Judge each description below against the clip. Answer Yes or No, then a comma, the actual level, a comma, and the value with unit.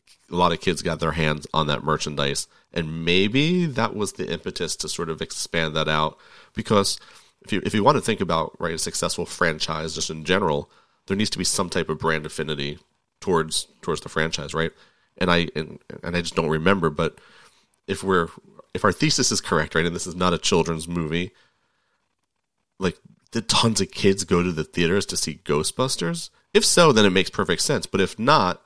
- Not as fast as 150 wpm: No, fast, 205 wpm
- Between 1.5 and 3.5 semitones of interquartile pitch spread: Yes, average, 2.9 semitones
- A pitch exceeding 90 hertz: No, very low, 85 Hz